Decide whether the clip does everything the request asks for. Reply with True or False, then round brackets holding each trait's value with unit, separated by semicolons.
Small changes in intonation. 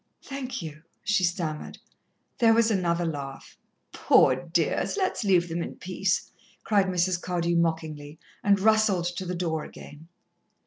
False (3.4 semitones)